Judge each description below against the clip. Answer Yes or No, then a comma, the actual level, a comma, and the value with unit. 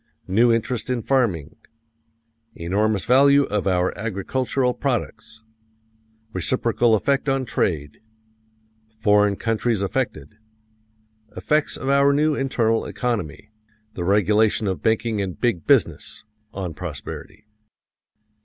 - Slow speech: Yes, slow, 105 wpm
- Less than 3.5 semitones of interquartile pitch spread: No, average, 4.7 semitones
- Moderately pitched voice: No, low, 110 Hz